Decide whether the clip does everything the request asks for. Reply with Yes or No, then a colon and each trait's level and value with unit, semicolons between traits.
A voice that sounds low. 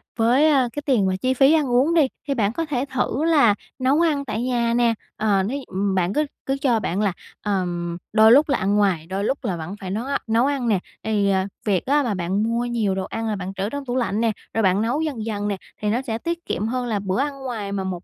No: high, 225 Hz